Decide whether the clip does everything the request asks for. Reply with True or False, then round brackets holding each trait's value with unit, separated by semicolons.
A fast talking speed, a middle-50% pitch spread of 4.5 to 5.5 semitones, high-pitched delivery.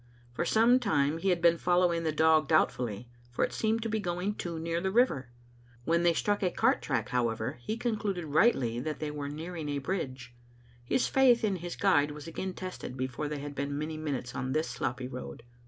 False (210 wpm; 5.1 semitones; 160 Hz)